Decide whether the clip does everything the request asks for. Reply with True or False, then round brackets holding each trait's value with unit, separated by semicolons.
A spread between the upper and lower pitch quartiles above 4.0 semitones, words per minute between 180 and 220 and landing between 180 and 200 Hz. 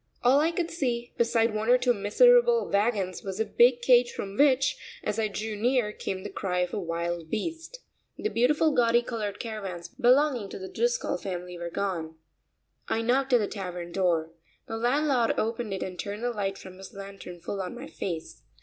False (4.5 semitones; 195 wpm; 220 Hz)